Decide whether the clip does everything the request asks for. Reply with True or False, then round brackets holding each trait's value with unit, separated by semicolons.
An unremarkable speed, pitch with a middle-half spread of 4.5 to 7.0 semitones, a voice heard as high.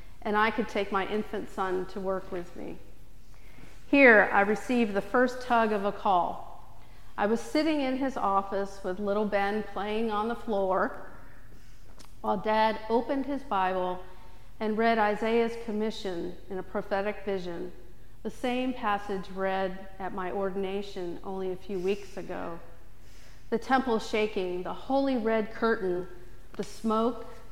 False (145 wpm; 3.2 semitones; 200 Hz)